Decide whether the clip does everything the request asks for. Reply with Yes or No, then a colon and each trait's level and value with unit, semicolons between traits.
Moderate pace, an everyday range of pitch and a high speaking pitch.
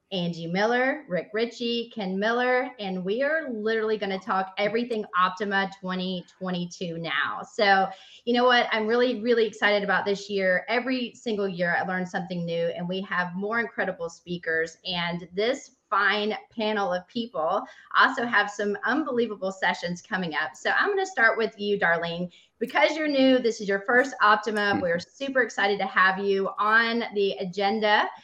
Yes: average, 170 wpm; average, 3.9 semitones; high, 205 Hz